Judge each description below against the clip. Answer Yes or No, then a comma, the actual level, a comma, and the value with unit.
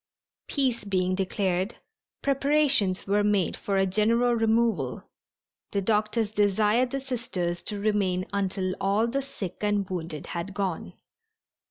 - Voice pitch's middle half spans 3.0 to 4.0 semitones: Yes, average, 3.6 semitones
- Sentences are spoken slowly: Yes, slow, 130 wpm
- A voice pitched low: No, high, 205 Hz